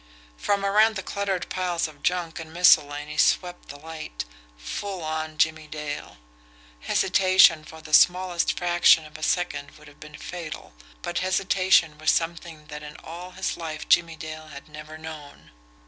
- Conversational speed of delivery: Yes, average, 160 wpm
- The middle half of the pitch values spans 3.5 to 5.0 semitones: No, average, 2.7 semitones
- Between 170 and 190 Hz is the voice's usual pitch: No, medium, 160 Hz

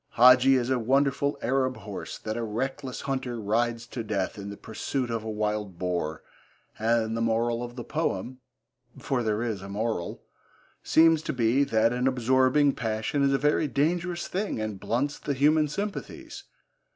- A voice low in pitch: Yes, low, 120 Hz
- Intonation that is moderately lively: Yes, average, 3.8 semitones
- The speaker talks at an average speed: Yes, average, 170 wpm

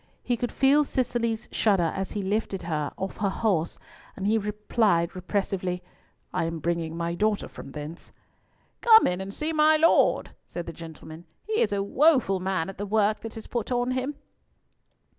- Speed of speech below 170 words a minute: No, average, 180 wpm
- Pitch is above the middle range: Yes, high, 200 Hz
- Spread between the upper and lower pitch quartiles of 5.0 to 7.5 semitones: Yes, wide, 5.6 semitones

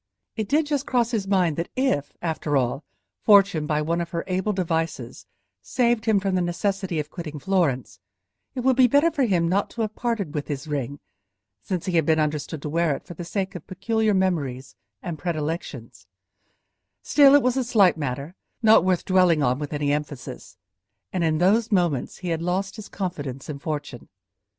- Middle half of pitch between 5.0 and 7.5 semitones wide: Yes, average, 5.3 semitones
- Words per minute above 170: Yes, average, 190 wpm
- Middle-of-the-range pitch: Yes, medium, 175 Hz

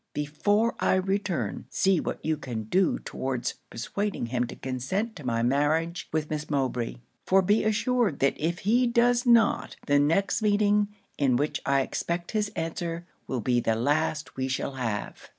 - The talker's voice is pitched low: No, medium, 160 Hz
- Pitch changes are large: Yes, wide, 7.5 semitones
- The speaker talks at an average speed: Yes, average, 170 wpm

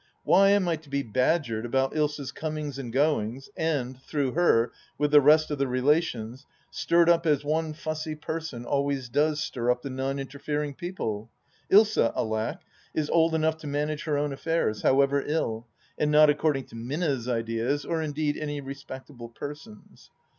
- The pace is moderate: Yes, average, 175 wpm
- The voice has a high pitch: No, medium, 145 Hz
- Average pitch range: Yes, average, 3.2 semitones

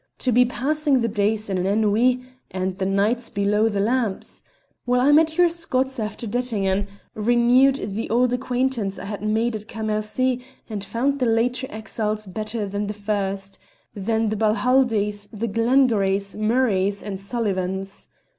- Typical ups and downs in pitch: Yes, average, 3.6 semitones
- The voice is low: No, high, 220 Hz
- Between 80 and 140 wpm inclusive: No, average, 160 wpm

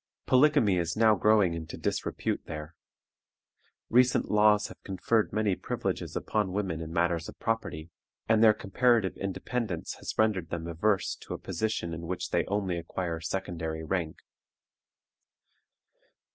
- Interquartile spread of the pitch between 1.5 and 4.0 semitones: No, average, 4.4 semitones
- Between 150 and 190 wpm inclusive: No, slow, 135 wpm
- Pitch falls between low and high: No, very low, 95 Hz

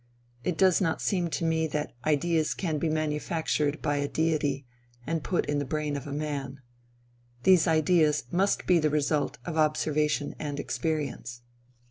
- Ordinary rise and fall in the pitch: No, narrow, 2.0 semitones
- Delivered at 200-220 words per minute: No, average, 155 wpm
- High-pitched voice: No, medium, 155 Hz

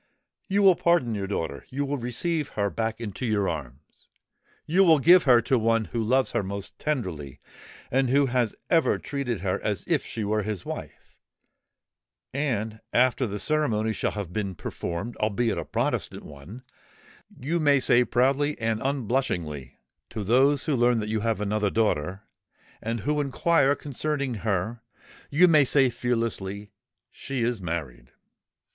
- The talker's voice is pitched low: Yes, low, 115 Hz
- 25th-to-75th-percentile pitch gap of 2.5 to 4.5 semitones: No, average, 5.1 semitones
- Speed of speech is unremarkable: Yes, average, 150 wpm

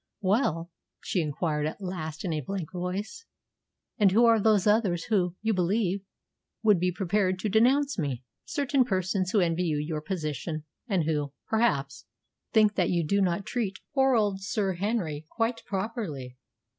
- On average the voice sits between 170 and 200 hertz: Yes, high, 190 Hz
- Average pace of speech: Yes, average, 160 wpm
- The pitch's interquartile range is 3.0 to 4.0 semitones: No, average, 4.7 semitones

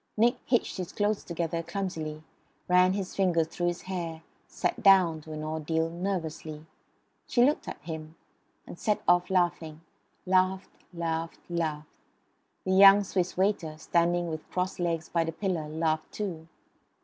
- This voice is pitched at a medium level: Yes, medium, 170 Hz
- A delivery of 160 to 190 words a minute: No, average, 150 wpm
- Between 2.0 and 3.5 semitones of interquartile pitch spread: Yes, average, 2.8 semitones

